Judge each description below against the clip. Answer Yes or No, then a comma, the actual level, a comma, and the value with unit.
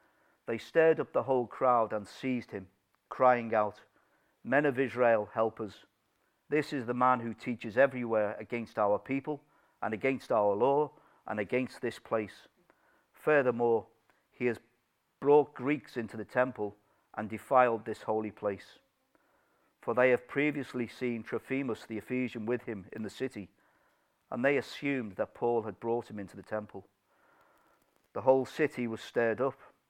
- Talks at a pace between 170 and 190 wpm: No, average, 155 wpm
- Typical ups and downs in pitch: Yes, average, 3.3 semitones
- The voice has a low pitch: Yes, low, 120 Hz